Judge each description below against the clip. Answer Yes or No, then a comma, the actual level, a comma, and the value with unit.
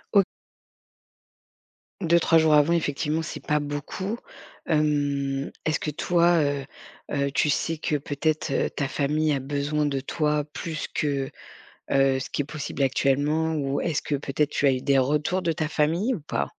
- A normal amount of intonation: No, narrow, 2.2 semitones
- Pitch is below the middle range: No, medium, 150 Hz